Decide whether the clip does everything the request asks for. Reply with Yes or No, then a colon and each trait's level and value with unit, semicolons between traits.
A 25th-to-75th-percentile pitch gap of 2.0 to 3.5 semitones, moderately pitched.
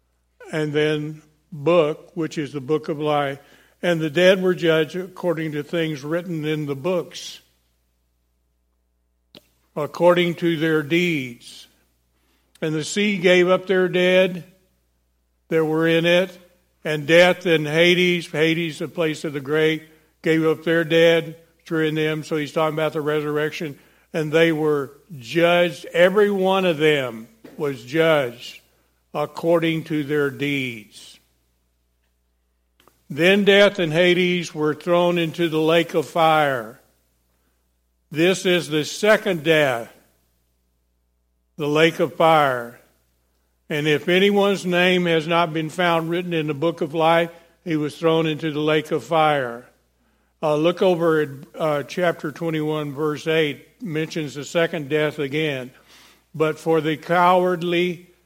Yes: average, 3.2 semitones; medium, 155 Hz